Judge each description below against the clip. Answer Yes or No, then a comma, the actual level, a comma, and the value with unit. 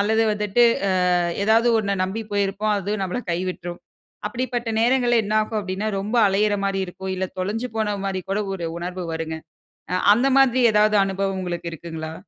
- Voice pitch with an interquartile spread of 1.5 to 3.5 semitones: Yes, average, 2.8 semitones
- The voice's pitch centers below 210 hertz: Yes, high, 200 Hz